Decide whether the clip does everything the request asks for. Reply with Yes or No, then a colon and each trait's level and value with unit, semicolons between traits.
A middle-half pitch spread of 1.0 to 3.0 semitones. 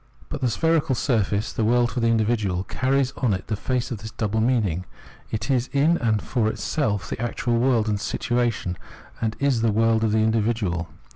Yes: average, 2.7 semitones